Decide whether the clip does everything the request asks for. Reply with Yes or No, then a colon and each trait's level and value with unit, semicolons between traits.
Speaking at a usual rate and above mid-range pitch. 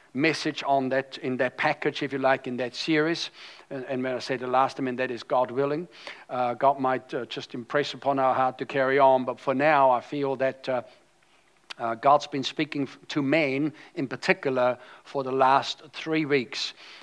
No: average, 195 wpm; low, 135 Hz